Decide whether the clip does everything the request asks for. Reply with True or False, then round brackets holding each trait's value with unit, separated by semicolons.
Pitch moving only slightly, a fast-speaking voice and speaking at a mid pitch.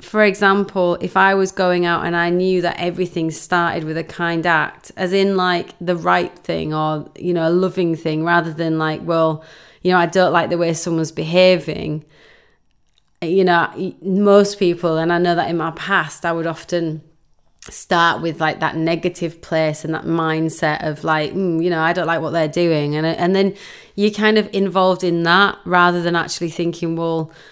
False (2.1 semitones; 195 wpm; 170 Hz)